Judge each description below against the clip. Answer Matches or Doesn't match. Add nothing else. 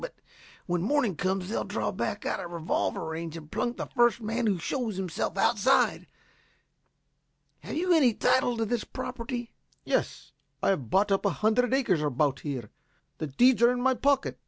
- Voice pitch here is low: Doesn't match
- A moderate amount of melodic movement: Doesn't match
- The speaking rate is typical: Matches